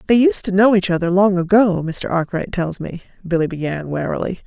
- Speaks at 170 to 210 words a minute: Yes, average, 200 wpm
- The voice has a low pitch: No, medium, 185 Hz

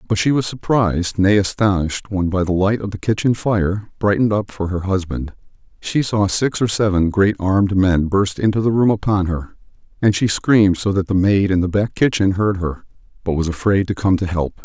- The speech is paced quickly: Yes, fast, 215 wpm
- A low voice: Yes, low, 100 Hz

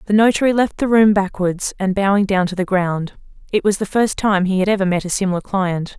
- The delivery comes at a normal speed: No, fast, 240 wpm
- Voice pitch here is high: Yes, high, 195 Hz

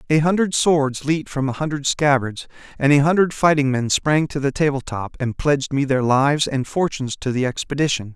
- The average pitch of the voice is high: No, medium, 140 Hz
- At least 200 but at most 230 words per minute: Yes, fast, 205 wpm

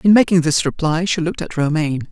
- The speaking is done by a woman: No, male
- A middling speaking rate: No, fast, 225 wpm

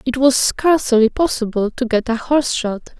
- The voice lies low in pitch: No, very high, 250 Hz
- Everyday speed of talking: Yes, average, 180 wpm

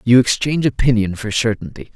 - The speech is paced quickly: No, average, 155 wpm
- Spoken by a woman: No, male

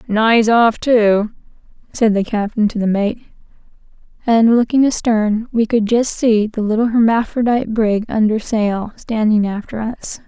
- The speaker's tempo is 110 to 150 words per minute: Yes, average, 145 wpm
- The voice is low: No, high, 220 Hz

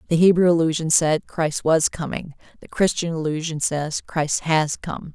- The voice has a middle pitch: Yes, medium, 160 Hz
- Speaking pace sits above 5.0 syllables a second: No, 4.6 syllables/s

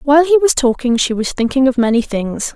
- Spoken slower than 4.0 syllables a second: No, 5.6 syllables/s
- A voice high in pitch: Yes, very high, 260 Hz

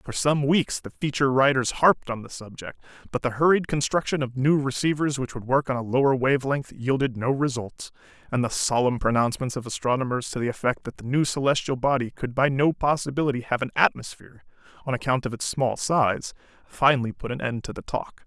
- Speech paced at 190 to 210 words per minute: Yes, fast, 205 wpm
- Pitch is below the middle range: Yes, low, 130 Hz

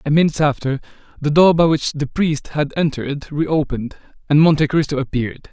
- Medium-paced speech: Yes, average, 175 wpm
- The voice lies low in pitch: No, medium, 150 Hz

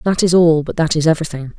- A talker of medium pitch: Yes, medium, 160 Hz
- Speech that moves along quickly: Yes, fast, 265 wpm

